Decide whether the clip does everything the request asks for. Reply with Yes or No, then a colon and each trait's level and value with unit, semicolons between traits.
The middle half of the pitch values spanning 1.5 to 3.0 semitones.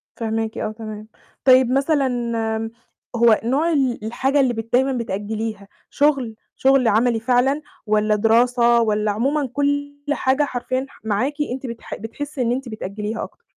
No: average, 3.5 semitones